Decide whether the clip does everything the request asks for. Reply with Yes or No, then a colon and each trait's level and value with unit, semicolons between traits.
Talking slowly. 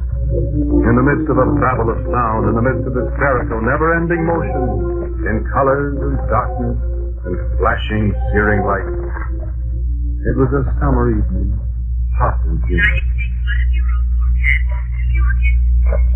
Yes: slow, 120 wpm